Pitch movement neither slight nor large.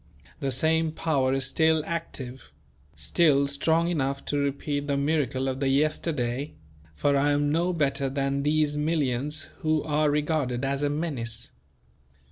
No: narrow, 2.3 semitones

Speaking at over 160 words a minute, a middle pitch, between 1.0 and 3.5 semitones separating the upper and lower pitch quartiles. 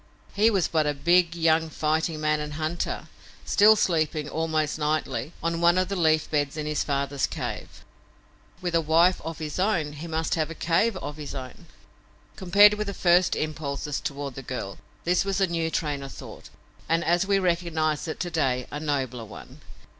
Yes: average, 190 wpm; medium, 160 Hz; average, 2.7 semitones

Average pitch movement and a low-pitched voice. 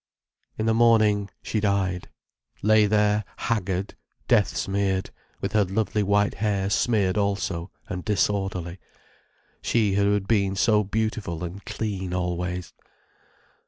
No: narrow, 2.1 semitones; low, 100 Hz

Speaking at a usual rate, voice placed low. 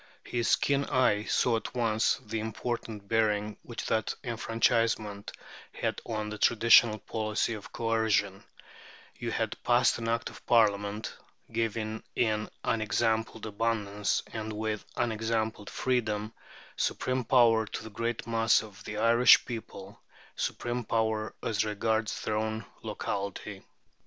No: slow, 125 wpm; low, 110 Hz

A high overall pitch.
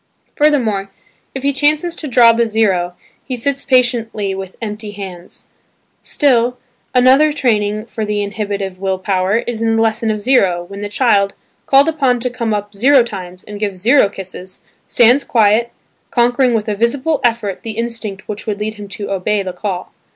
Yes: high, 220 Hz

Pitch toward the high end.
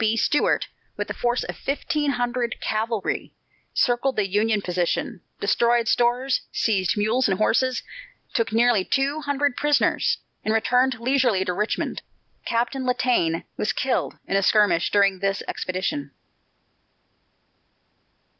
Yes: high, 230 Hz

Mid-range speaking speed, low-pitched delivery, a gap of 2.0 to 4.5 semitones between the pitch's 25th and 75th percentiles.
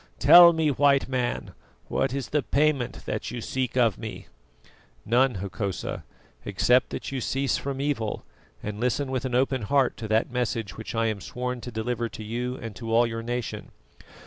Yes: average, 180 wpm; low, 125 Hz; average, 2.8 semitones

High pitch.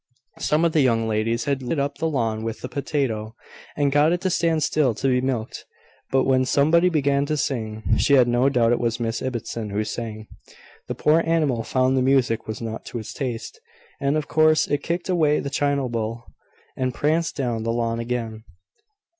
No: low, 130 Hz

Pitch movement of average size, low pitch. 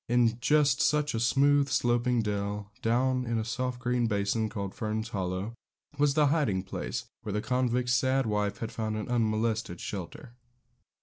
Yes: average, 3.2 semitones; low, 115 Hz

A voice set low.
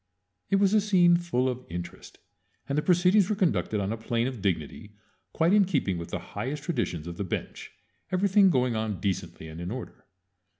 Yes: low, 125 Hz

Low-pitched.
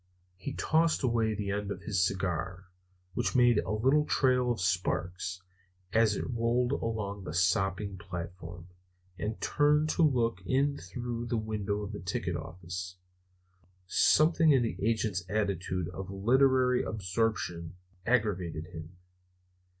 Yes: low, 105 Hz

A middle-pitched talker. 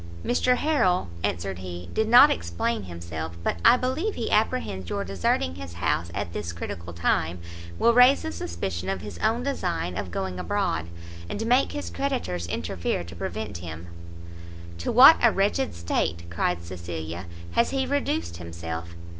No: very low, 90 Hz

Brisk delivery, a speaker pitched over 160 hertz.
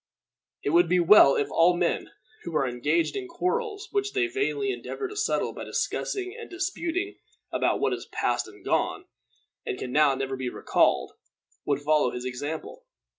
No: average, 175 wpm; medium, 185 Hz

